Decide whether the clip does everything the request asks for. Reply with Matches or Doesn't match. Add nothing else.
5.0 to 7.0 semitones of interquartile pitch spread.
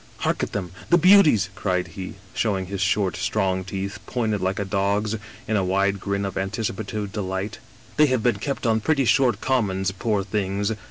Doesn't match